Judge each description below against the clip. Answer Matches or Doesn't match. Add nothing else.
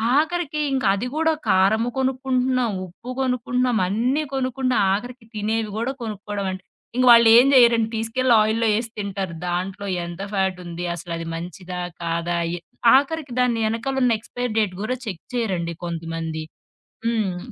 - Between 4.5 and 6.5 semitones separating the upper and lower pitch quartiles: Matches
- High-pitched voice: Matches